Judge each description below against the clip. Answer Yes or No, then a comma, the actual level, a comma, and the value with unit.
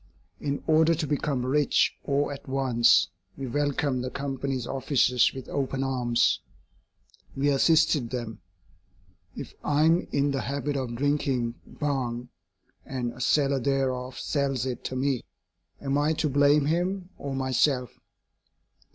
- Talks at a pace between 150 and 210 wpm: No, slow, 135 wpm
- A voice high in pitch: No, low, 135 Hz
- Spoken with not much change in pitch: Yes, narrow, 2.1 semitones